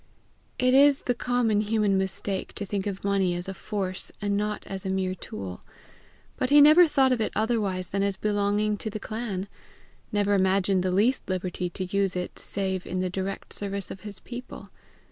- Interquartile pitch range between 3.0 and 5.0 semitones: No, narrow, 2.4 semitones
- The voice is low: No, high, 200 Hz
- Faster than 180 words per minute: Yes, average, 190 wpm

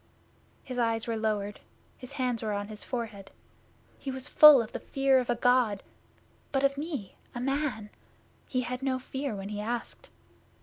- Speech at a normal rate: Yes, average, 175 wpm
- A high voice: Yes, high, 245 Hz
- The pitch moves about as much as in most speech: Yes, average, 3.6 semitones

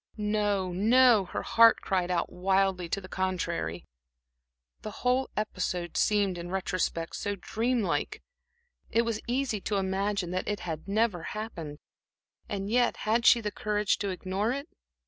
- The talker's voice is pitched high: Yes, high, 200 Hz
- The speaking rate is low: No, average, 155 wpm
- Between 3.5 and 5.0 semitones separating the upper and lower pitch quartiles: No, average, 3.1 semitones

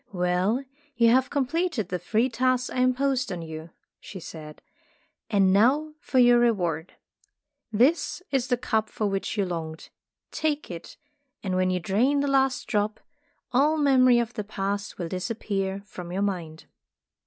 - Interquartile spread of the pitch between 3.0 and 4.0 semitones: No, wide, 5.6 semitones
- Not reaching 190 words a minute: Yes, average, 160 wpm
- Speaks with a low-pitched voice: No, high, 215 Hz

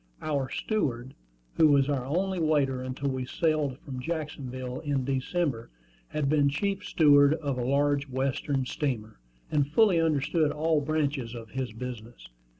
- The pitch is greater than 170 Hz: No, medium, 140 Hz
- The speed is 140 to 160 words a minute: Yes, average, 150 wpm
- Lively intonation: No, average, 3.1 semitones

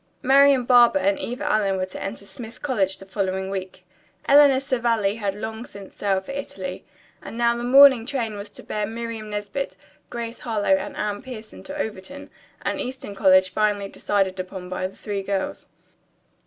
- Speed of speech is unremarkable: Yes, average, 175 wpm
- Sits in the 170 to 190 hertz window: No, high, 210 Hz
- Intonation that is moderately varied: Yes, average, 3.8 semitones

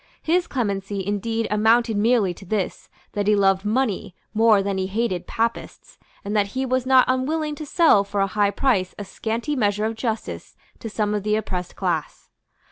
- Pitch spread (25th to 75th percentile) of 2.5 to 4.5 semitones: Yes, average, 3.1 semitones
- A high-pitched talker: Yes, high, 215 Hz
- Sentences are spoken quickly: No, average, 185 wpm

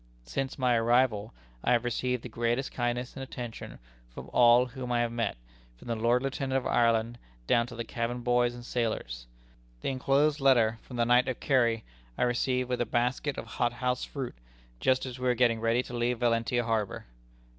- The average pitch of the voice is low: Yes, low, 120 Hz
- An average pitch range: No, narrow, 1.4 semitones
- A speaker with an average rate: Yes, average, 190 wpm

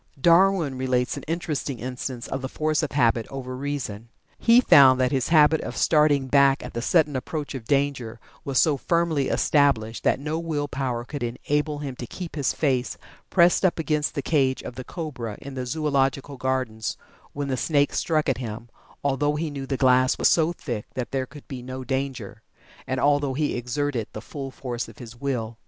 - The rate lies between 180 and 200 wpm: Yes, average, 195 wpm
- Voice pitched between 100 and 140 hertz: Yes, low, 135 Hz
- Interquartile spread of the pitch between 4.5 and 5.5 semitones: No, average, 2.8 semitones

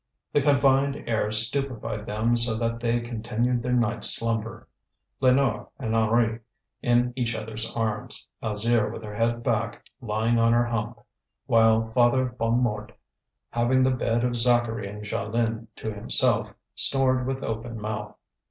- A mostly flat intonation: Yes, narrow, 1.6 semitones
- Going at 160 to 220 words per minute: No, average, 145 wpm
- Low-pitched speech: Yes, low, 115 Hz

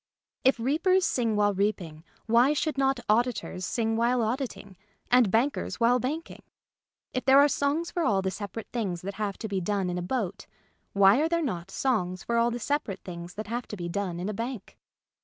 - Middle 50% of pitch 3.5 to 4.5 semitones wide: No, average, 4.9 semitones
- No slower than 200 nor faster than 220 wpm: Yes, fast, 205 wpm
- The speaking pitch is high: Yes, high, 225 Hz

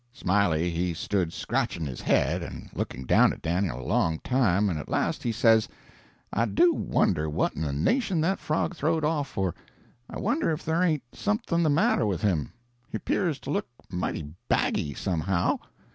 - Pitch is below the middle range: Yes, low, 105 Hz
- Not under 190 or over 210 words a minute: No, average, 180 wpm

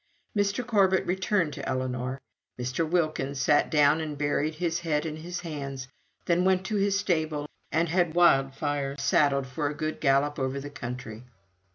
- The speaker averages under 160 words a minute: No, average, 165 wpm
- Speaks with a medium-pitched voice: Yes, medium, 150 Hz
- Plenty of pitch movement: No, average, 4.1 semitones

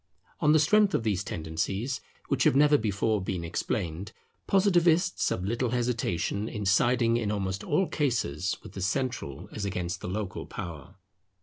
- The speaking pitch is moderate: No, low, 105 Hz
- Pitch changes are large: Yes, wide, 5.8 semitones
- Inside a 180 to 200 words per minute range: No, average, 160 wpm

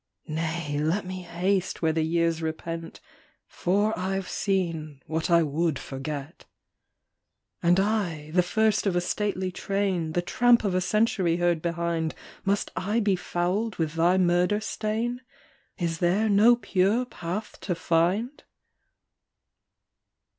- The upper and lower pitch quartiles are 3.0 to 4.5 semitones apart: Yes, average, 3.5 semitones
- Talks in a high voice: No, medium, 180 Hz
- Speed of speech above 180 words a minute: No, average, 140 wpm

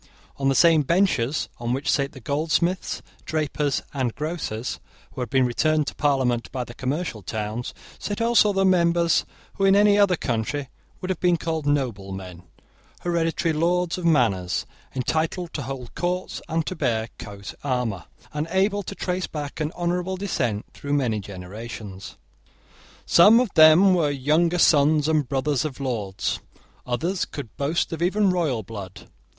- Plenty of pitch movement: Yes, wide, 6.0 semitones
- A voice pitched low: No, medium, 150 Hz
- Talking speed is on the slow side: No, average, 155 wpm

